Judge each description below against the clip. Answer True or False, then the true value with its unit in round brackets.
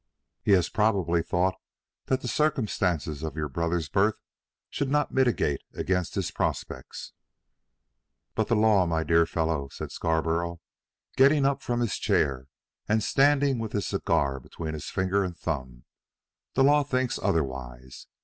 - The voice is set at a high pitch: False (90 Hz)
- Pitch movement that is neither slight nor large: False (7.1 semitones)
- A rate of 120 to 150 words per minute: True (145 wpm)